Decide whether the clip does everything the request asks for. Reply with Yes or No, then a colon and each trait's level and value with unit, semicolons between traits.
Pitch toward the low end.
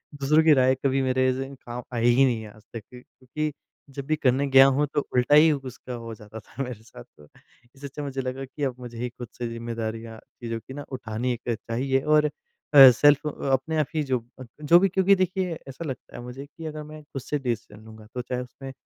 Yes: low, 130 Hz